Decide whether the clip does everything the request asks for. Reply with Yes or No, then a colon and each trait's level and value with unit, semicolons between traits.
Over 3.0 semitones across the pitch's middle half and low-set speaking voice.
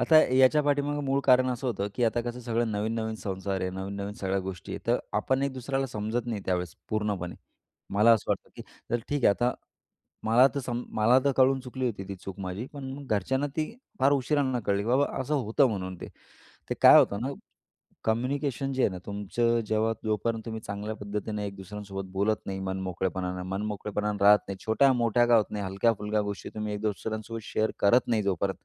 Yes: average, 4.0 semitones; low, 110 Hz